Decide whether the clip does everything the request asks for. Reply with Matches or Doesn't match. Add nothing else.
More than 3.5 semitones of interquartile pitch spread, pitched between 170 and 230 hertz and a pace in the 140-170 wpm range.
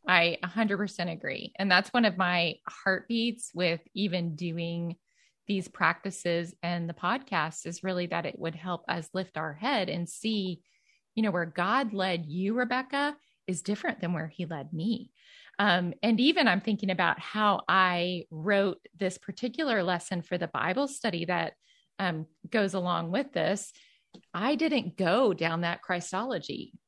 Matches